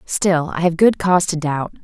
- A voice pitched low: No, medium, 170 Hz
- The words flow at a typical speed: No, fast, 230 wpm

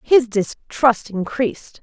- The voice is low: No, high, 230 Hz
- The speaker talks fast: No, slow, 100 wpm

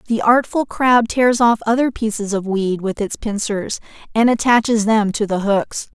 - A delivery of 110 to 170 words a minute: No, average, 180 wpm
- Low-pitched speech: No, high, 220 Hz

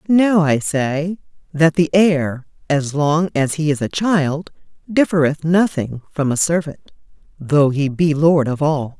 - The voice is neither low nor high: Yes, medium, 155 Hz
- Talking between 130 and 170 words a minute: Yes, average, 160 wpm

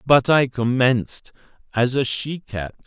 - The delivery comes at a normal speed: Yes, average, 145 wpm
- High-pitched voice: No, low, 125 Hz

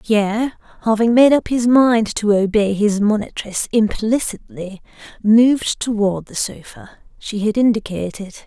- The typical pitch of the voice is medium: No, high, 215 Hz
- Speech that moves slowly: Yes, slow, 130 wpm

